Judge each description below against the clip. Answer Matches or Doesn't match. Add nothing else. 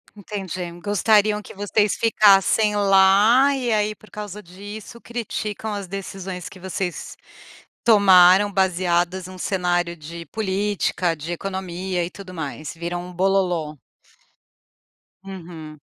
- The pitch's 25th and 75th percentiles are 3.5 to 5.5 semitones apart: Doesn't match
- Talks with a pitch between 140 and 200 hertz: Matches